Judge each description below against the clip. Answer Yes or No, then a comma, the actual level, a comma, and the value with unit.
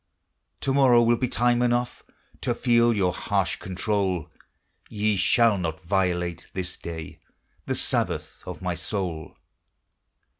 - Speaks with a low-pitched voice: Yes, very low, 95 Hz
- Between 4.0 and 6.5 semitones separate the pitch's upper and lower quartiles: Yes, average, 5.1 semitones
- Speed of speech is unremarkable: No, slow, 125 wpm